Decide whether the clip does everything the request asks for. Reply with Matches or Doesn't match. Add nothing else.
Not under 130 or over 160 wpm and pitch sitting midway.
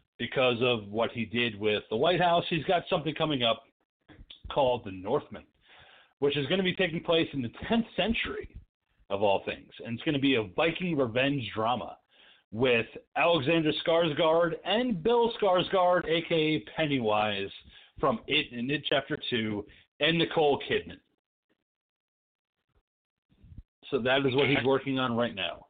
Matches